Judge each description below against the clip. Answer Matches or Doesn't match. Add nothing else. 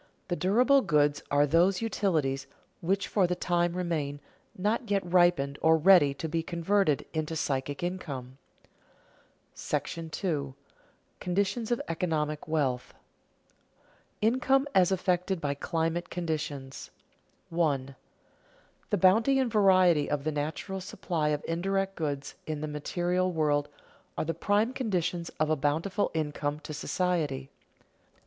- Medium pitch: Matches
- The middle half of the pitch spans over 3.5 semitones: Matches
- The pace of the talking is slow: Matches